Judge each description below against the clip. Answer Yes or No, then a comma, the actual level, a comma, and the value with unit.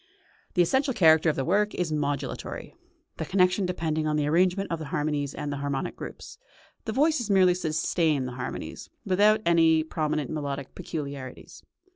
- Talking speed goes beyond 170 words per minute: No, average, 160 wpm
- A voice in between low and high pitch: Yes, medium, 160 Hz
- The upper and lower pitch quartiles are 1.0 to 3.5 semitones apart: No, average, 4.0 semitones